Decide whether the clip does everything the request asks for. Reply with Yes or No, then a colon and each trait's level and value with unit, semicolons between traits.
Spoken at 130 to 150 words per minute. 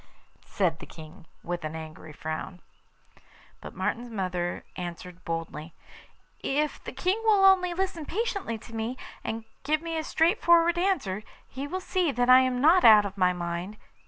No: average, 160 wpm